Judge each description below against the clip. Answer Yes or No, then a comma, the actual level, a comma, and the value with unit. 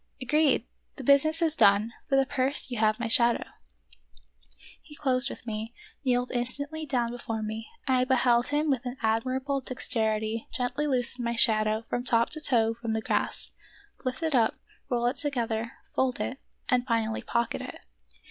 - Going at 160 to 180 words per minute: Yes, average, 175 wpm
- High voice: Yes, high, 245 Hz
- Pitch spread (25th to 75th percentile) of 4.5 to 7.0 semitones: No, average, 2.8 semitones